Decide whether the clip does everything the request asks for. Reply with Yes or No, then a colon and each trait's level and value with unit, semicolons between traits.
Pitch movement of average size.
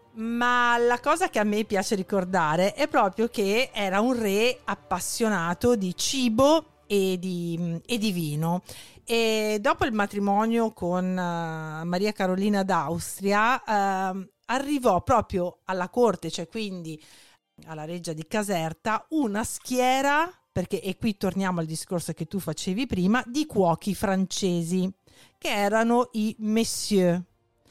Yes: average, 4.3 semitones